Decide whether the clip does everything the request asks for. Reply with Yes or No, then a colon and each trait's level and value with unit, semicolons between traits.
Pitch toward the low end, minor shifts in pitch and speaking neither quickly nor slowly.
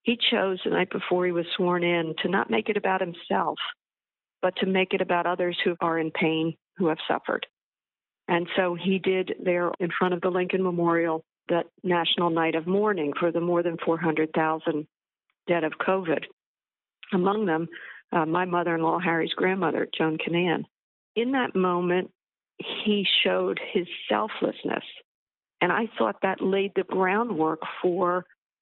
No: medium, 175 Hz; narrow, 2.2 semitones; average, 160 wpm